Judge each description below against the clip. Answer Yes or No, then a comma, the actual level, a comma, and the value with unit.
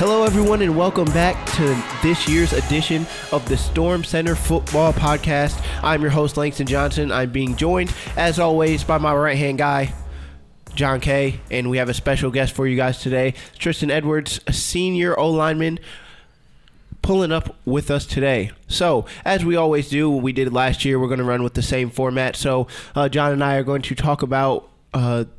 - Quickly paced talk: No, average, 195 wpm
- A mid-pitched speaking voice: Yes, medium, 145 Hz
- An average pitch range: Yes, average, 3.5 semitones